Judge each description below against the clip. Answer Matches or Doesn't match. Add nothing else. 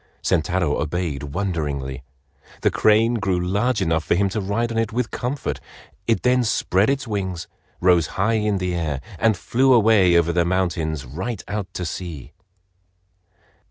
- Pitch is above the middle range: Doesn't match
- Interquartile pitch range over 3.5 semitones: Matches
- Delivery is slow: Doesn't match